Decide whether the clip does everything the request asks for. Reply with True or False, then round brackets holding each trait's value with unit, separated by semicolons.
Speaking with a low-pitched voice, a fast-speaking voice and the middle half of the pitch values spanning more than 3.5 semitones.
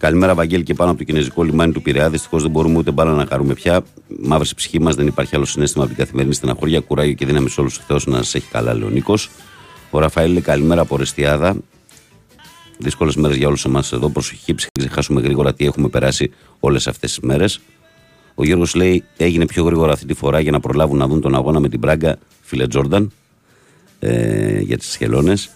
False (75 Hz; 205 wpm; 2.8 semitones)